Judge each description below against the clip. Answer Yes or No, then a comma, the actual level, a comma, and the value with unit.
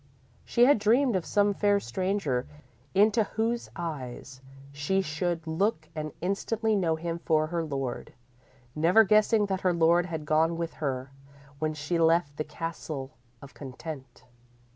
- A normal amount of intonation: Yes, average, 4.7 semitones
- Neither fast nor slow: Yes, average, 145 wpm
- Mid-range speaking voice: Yes, medium, 165 Hz